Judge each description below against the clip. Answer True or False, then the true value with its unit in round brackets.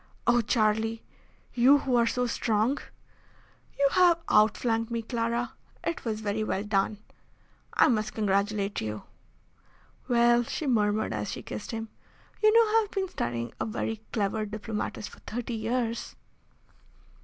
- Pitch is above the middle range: True (225 Hz)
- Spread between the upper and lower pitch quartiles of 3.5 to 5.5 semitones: False (2.4 semitones)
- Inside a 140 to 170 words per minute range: True (145 wpm)